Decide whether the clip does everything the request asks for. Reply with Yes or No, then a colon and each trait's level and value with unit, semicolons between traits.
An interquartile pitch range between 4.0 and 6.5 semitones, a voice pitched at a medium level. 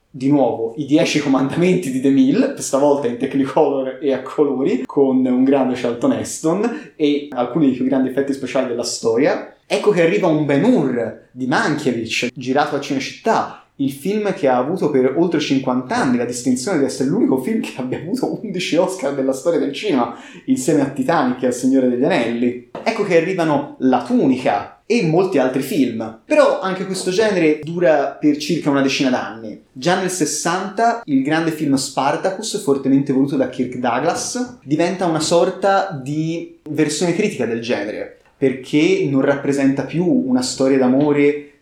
Yes: average, 4.8 semitones; medium, 145 Hz